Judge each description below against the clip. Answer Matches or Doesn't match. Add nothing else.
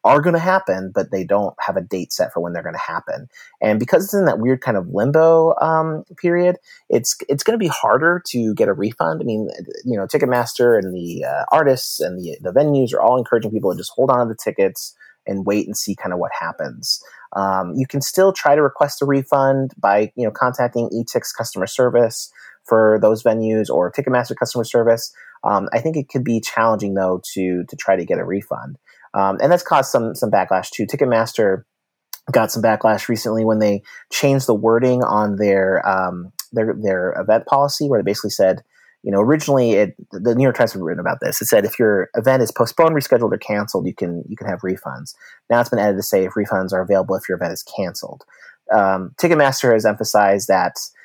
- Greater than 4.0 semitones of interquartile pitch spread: Matches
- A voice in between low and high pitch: Doesn't match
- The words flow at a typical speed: Doesn't match